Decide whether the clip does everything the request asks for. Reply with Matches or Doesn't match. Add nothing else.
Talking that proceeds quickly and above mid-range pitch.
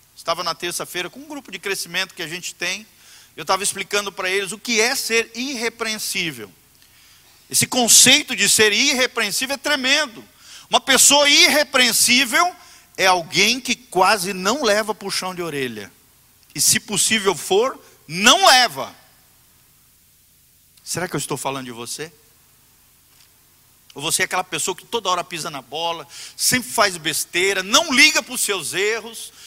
Doesn't match